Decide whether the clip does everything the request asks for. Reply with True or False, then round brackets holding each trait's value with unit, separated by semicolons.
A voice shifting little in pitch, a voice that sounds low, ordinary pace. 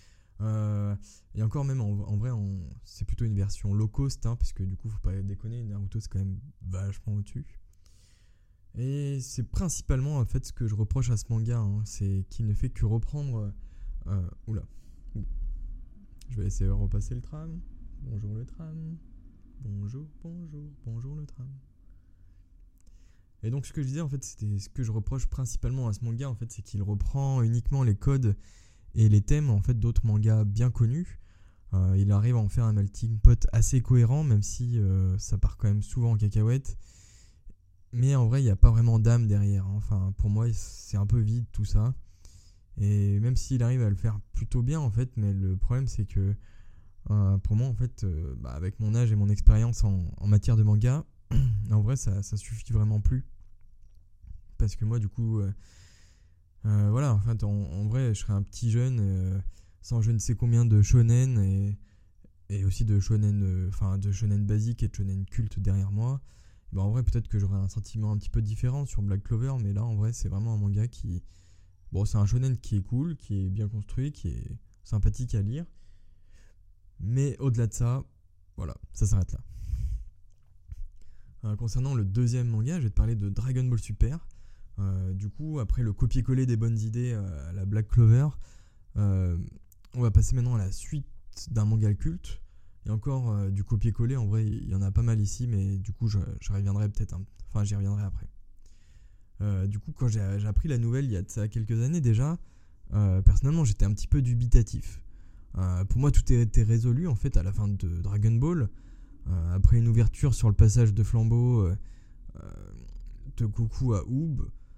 False (3.4 semitones; 105 Hz; 200 wpm)